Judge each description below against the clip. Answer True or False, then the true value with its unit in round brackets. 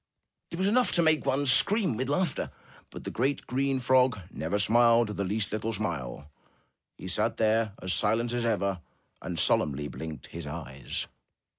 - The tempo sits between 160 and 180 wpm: True (165 wpm)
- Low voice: True (110 Hz)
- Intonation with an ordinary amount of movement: False (6.2 semitones)